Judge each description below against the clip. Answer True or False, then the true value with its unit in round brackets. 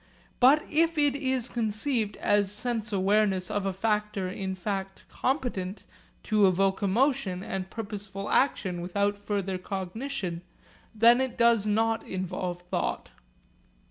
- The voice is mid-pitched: False (205 Hz)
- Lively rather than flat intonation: False (3.6 semitones)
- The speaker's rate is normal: False (125 wpm)